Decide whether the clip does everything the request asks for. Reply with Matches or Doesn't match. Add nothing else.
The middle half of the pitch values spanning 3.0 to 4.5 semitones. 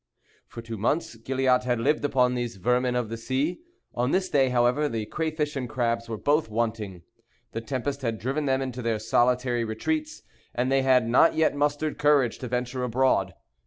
Matches